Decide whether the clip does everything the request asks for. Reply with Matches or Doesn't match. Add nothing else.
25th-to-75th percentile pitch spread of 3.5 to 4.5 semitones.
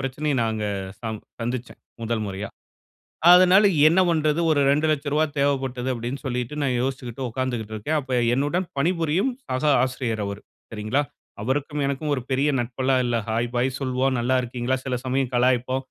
Doesn't match